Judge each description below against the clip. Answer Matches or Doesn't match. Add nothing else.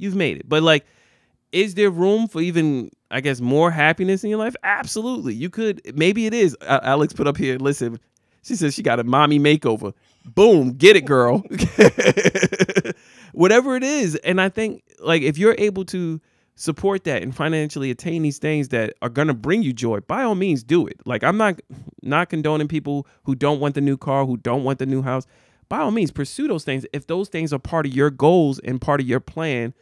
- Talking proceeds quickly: Matches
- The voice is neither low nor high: Matches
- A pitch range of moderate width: Doesn't match